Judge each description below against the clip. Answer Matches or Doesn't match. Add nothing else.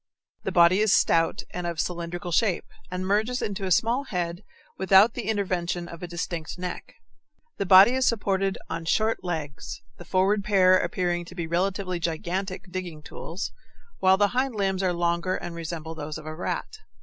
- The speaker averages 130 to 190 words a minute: Matches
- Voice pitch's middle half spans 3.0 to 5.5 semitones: Doesn't match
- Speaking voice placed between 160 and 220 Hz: Matches